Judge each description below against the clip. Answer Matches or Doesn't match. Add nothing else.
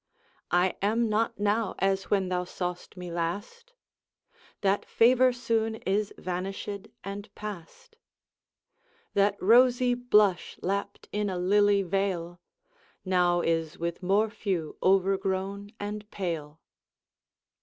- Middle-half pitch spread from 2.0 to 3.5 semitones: Matches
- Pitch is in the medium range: Doesn't match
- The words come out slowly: Matches